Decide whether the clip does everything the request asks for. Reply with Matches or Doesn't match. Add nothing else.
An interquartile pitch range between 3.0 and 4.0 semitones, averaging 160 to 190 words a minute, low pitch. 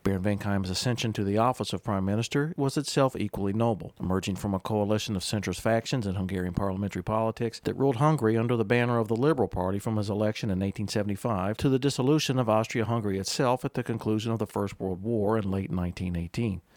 Doesn't match